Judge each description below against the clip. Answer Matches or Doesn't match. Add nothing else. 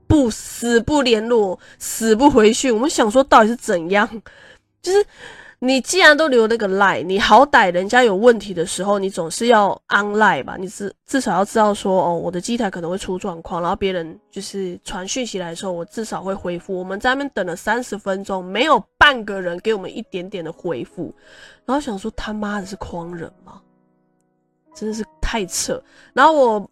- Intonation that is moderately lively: Matches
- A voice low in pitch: Doesn't match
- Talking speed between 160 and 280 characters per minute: Doesn't match